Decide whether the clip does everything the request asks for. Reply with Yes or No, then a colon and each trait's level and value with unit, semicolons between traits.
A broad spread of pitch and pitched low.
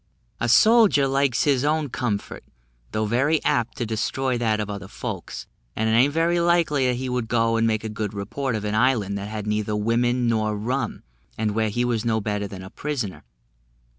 No: average, 3.8 semitones; low, 115 Hz